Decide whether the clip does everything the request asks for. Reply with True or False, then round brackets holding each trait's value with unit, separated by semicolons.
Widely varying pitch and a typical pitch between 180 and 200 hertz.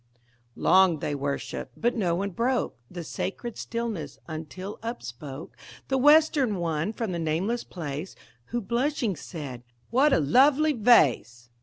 True (7.6 semitones; 190 Hz)